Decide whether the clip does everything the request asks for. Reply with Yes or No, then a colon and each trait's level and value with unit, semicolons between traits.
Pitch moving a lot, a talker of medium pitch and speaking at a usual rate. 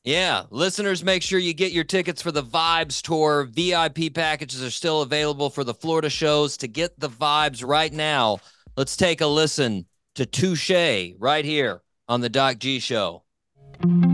No: average, 3.7 semitones; medium, 150 Hz; average, 170 wpm